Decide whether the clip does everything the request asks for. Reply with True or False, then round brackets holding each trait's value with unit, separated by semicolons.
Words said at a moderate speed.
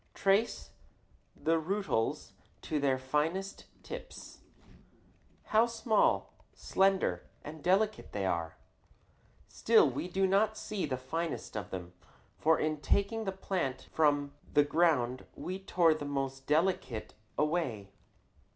False (120 wpm)